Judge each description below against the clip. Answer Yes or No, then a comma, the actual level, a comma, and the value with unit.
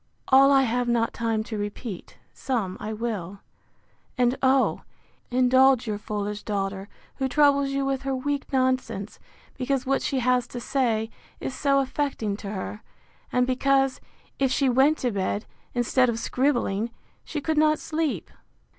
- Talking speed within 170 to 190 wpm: No, average, 155 wpm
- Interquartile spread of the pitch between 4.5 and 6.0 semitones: No, average, 3.7 semitones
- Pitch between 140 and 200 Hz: No, very high, 250 Hz